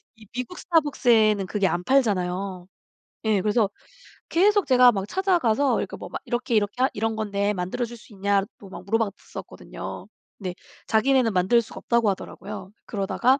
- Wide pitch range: No, average, 3.9 semitones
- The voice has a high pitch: Yes, high, 220 Hz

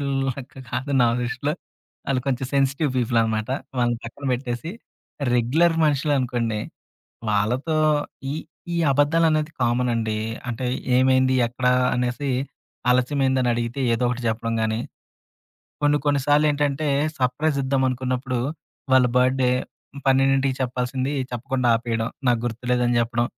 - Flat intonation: Yes, narrow, 2.3 semitones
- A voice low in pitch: Yes, low, 125 Hz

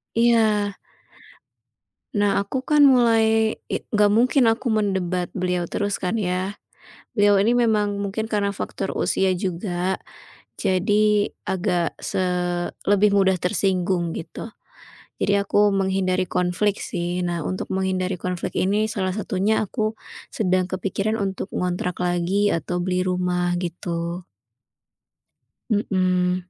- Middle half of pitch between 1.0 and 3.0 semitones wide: Yes, narrow, 2.5 semitones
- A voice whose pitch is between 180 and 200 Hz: Yes, high, 190 Hz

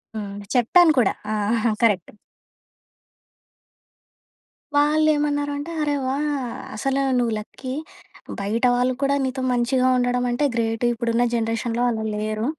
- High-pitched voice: Yes, high, 245 Hz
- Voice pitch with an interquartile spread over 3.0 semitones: Yes, average, 3.7 semitones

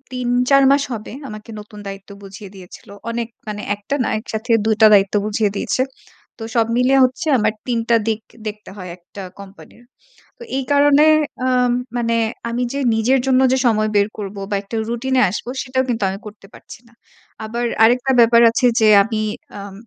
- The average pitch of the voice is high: Yes, high, 225 Hz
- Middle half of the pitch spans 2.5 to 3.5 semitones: Yes, average, 3.2 semitones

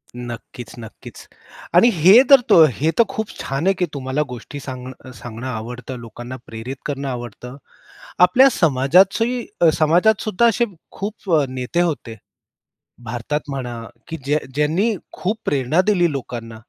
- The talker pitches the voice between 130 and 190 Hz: Yes, medium, 140 Hz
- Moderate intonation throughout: No, wide, 6.7 semitones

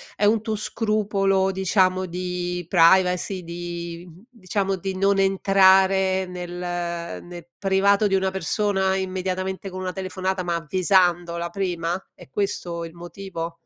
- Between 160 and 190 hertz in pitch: Yes, medium, 185 Hz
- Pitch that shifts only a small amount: Yes, narrow, 1.8 semitones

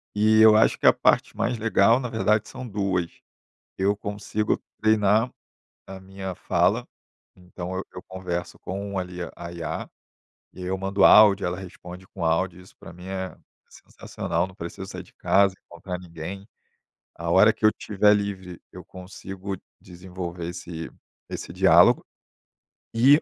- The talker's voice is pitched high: No, very low, 95 Hz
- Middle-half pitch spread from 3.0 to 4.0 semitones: No, narrow, 2.4 semitones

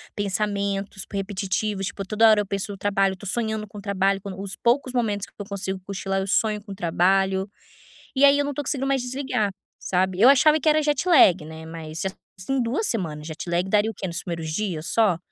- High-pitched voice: Yes, high, 200 Hz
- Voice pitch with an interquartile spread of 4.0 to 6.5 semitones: No, average, 3.3 semitones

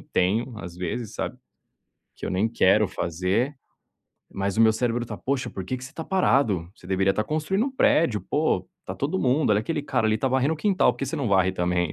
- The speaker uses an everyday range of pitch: No, wide, 6.6 semitones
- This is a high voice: No, low, 115 Hz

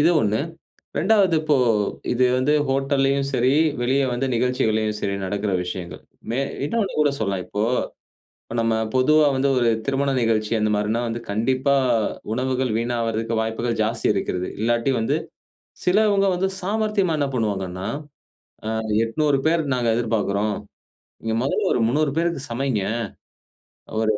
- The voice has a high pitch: No, low, 120 Hz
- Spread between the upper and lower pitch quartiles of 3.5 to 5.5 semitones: Yes, average, 4.2 semitones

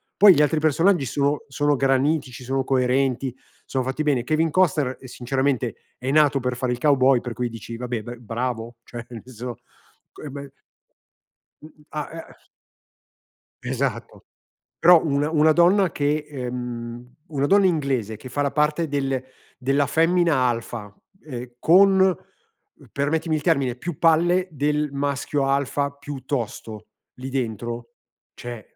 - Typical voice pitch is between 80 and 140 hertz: Yes, low, 135 Hz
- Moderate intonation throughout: Yes, average, 3.4 semitones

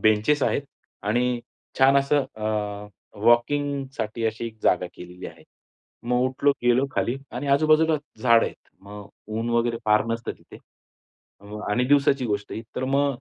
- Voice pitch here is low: Yes, low, 120 Hz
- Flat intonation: No, average, 4.0 semitones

